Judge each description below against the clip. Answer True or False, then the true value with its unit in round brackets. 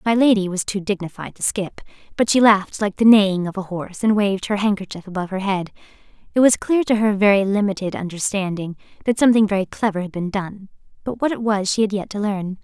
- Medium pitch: False (200 Hz)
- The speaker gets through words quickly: True (225 wpm)